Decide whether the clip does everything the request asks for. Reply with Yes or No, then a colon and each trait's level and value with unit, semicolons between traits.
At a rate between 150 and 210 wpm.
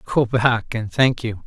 Yes: fast, 205 wpm